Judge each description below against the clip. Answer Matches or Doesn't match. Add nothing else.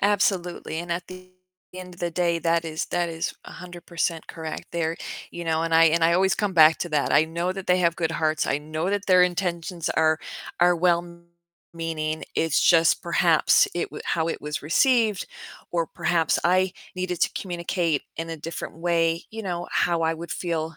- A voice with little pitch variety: Matches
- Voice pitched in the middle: Matches